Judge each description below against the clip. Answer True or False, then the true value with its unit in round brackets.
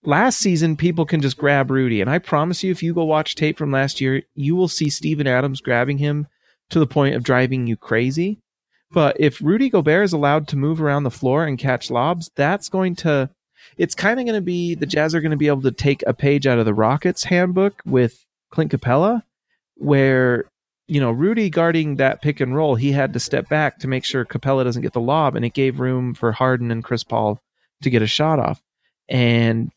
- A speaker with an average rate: False (225 wpm)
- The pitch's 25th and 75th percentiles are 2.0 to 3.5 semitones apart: False (4.2 semitones)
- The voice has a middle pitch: True (145 Hz)